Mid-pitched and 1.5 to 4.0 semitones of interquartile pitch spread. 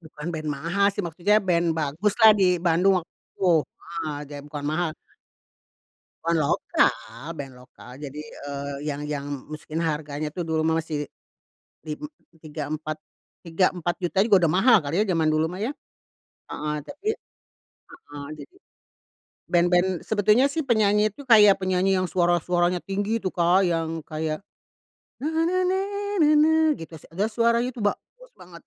No: medium, 175 Hz; average, 4.7 semitones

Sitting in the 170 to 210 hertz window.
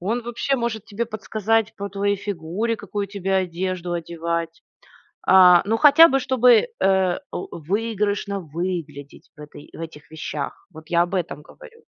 Yes: high, 190 Hz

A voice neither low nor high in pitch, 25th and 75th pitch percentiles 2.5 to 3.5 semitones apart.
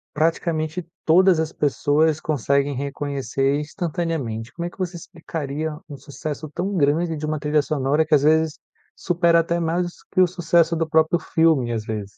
Yes: medium, 155 Hz; average, 2.8 semitones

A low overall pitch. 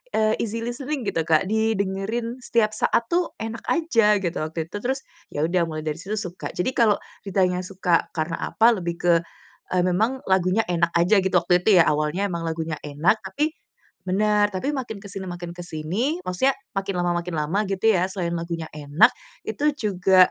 No: high, 190 Hz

